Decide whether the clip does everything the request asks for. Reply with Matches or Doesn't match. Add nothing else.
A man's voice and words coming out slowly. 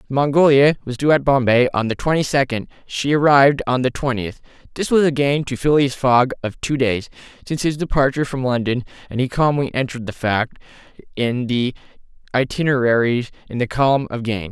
Doesn't match